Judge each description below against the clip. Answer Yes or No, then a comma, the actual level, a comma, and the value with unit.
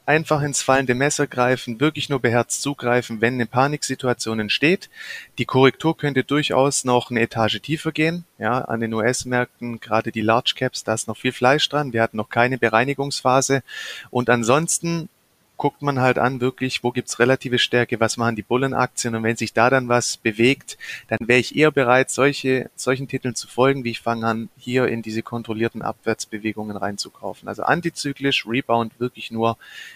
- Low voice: Yes, low, 125 Hz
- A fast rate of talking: No, average, 180 wpm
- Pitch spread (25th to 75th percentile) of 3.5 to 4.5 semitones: No, average, 2.9 semitones